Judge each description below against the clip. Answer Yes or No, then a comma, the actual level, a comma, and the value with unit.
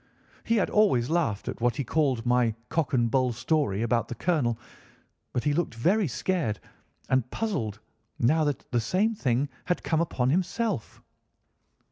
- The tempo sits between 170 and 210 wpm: No, average, 160 wpm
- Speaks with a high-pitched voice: No, low, 135 Hz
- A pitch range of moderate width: No, wide, 6.5 semitones